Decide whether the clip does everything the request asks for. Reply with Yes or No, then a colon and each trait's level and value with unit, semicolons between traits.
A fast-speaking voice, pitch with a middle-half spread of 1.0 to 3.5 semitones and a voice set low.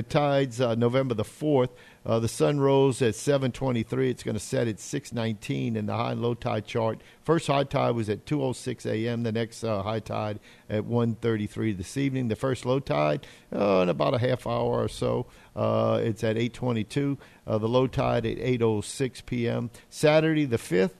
Yes: fast, 225 wpm; average, 3.2 semitones; low, 120 Hz